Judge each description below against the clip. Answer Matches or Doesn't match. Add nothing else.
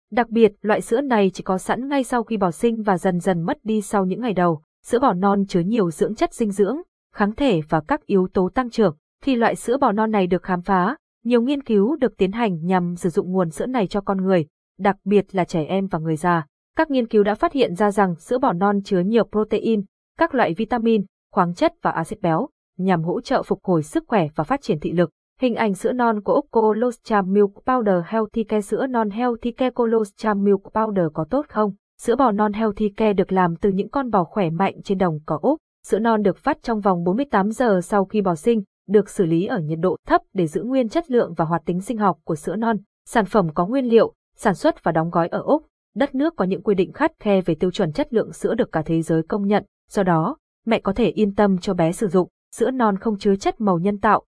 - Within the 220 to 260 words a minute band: Matches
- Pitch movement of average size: Matches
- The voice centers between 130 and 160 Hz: Doesn't match